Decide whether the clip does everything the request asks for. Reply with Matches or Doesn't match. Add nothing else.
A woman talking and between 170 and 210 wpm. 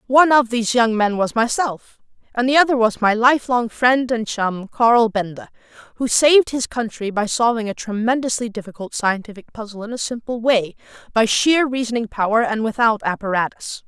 Matches